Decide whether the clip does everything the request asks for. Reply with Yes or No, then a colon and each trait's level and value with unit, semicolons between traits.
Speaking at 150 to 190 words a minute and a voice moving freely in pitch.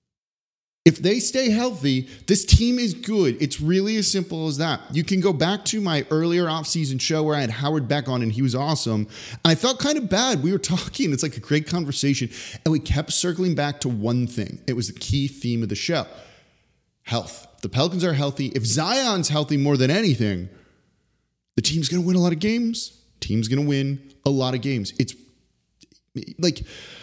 No: average, 200 wpm; wide, 5.7 semitones